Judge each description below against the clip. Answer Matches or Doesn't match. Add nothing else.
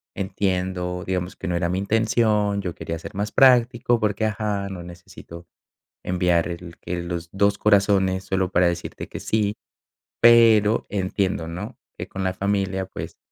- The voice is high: Doesn't match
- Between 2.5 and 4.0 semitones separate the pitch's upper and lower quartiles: Matches